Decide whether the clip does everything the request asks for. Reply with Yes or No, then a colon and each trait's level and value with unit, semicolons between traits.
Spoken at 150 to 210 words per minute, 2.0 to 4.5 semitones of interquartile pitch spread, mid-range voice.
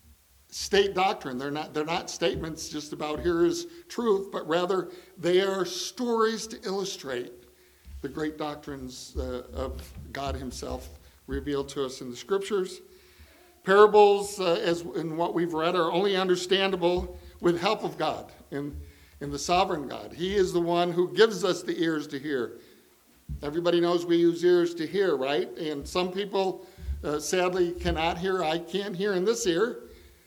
No: average, 165 wpm; average, 4.9 semitones; medium, 175 Hz